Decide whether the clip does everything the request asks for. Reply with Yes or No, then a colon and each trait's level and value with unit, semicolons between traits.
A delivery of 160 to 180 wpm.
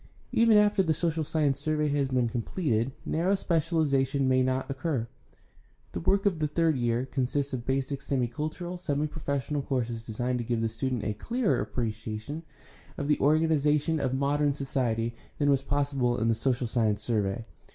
Yes: average, 170 wpm